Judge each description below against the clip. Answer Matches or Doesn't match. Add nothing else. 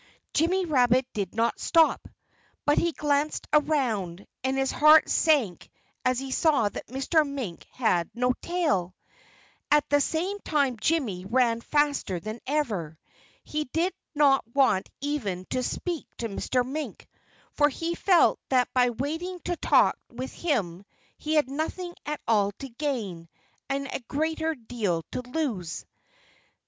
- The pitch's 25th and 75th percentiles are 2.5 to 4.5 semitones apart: Doesn't match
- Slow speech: Doesn't match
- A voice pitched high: Matches